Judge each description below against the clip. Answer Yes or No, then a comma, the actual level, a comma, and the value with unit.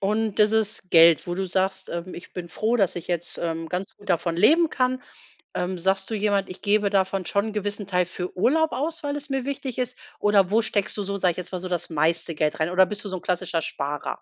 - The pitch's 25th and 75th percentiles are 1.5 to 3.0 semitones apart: No, average, 3.4 semitones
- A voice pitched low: No, high, 195 Hz